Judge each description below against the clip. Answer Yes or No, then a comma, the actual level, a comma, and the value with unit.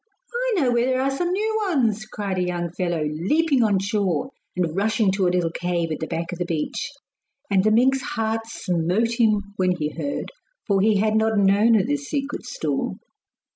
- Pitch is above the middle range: Yes, high, 210 Hz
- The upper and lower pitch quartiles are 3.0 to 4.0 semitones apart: No, average, 5.1 semitones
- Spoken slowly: No, average, 200 wpm